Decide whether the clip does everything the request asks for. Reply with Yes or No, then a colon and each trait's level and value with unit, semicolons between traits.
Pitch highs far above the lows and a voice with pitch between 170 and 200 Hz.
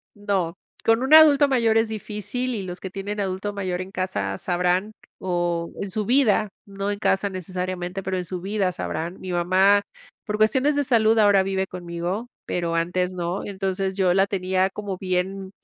No: narrow, 2.5 semitones; high, 190 Hz